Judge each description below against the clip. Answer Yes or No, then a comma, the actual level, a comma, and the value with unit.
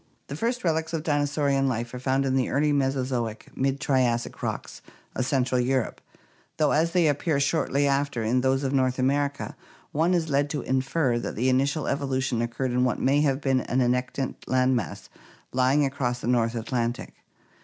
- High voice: No, low, 135 Hz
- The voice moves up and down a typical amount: No, narrow, 2.2 semitones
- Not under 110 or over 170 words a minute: No, average, 180 wpm